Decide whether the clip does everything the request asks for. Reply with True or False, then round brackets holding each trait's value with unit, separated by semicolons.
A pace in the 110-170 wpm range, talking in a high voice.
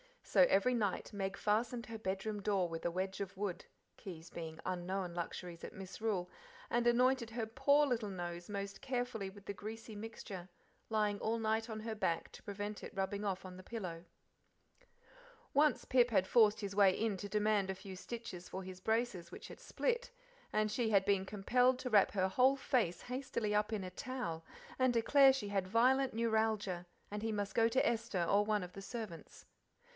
False (190 wpm; 210 Hz)